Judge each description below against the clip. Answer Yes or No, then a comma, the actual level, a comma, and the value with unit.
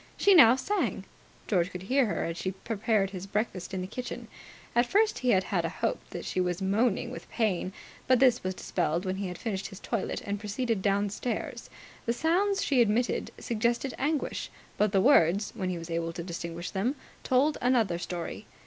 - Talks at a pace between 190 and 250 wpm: Yes, average, 195 wpm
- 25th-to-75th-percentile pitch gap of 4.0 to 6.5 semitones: Yes, average, 5.1 semitones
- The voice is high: Yes, high, 205 Hz